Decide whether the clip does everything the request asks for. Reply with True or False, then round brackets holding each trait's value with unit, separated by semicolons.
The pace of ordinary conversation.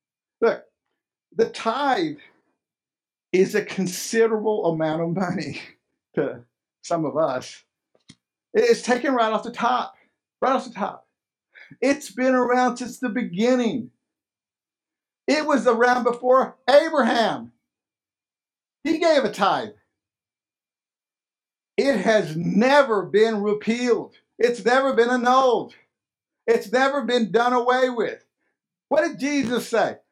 False (115 wpm)